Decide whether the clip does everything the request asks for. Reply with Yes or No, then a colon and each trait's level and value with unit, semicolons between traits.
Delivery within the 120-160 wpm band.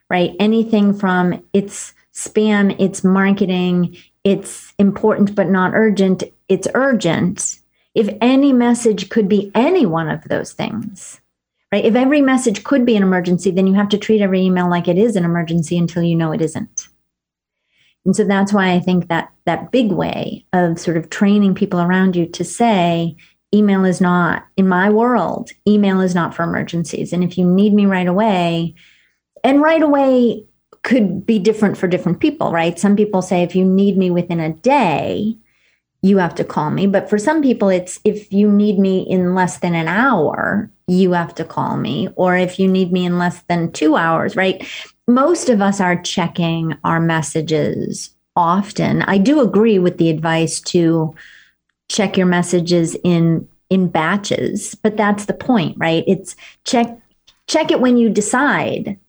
No: average, 175 wpm